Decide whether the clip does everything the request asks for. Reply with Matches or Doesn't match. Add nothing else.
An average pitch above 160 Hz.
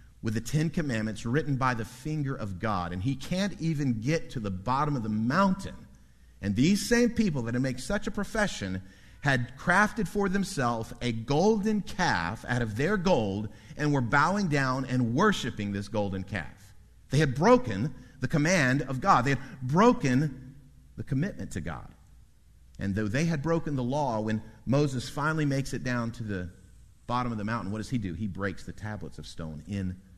Doesn't match